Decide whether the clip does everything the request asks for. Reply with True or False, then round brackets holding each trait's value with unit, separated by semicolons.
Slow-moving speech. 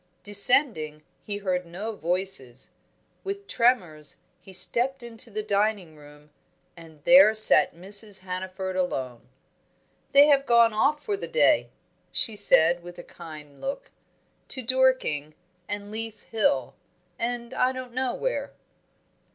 True (130 wpm)